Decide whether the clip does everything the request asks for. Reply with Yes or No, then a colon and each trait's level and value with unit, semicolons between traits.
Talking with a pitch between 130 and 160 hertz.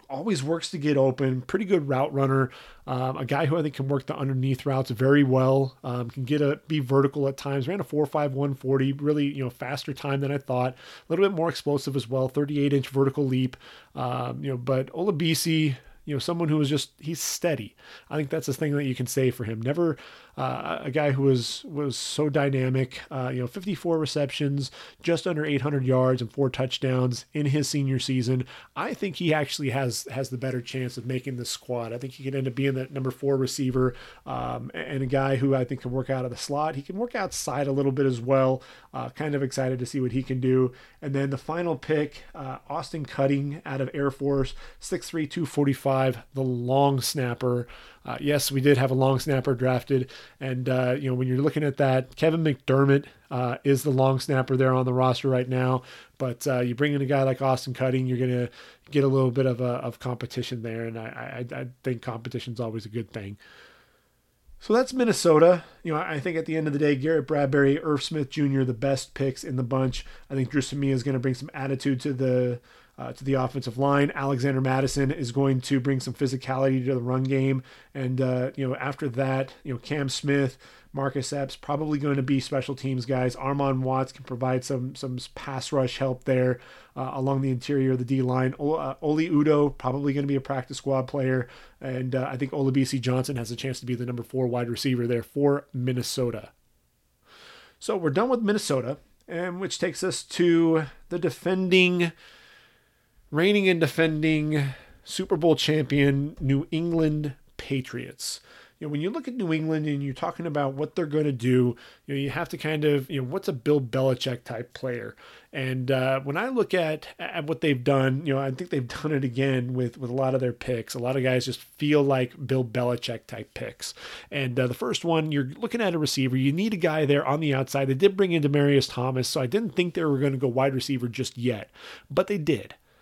Yes: low, 135 Hz